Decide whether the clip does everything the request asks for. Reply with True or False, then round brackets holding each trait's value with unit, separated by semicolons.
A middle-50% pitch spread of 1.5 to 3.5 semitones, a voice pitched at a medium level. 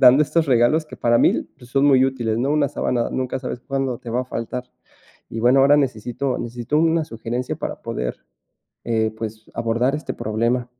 False (2.8 semitones; 125 Hz)